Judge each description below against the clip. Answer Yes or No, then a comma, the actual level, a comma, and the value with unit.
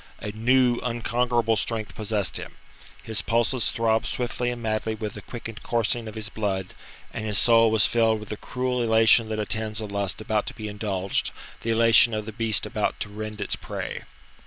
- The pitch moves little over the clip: Yes, narrow, 1.6 semitones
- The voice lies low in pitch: Yes, low, 110 Hz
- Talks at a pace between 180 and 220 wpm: Yes, average, 190 wpm